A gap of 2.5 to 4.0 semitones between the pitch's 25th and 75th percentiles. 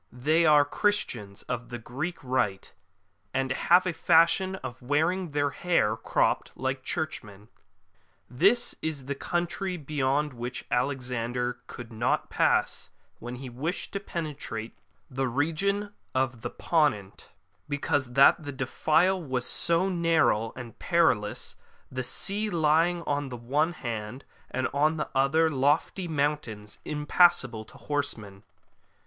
No: average, 5.1 semitones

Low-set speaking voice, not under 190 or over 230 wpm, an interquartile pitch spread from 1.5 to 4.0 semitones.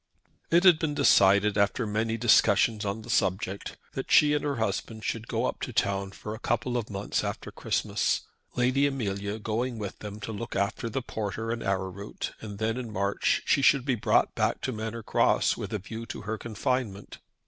Yes: low, 110 Hz; average, 195 wpm; average, 3.2 semitones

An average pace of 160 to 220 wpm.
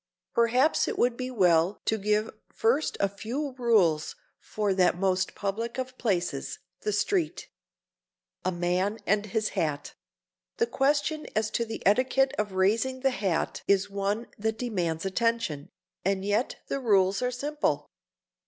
No: average, 145 wpm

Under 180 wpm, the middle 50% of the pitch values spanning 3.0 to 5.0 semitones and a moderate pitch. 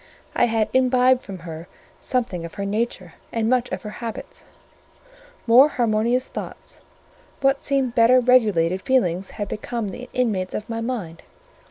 No: average, 150 wpm; average, 4.2 semitones; high, 230 Hz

